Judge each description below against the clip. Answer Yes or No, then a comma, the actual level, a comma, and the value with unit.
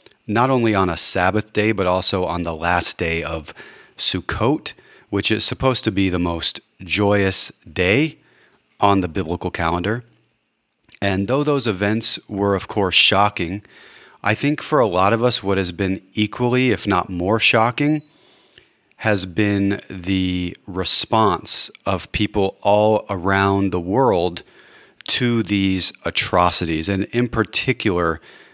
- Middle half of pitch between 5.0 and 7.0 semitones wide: No, average, 3.3 semitones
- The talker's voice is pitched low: Yes, low, 100 Hz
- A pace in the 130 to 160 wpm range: Yes, average, 140 wpm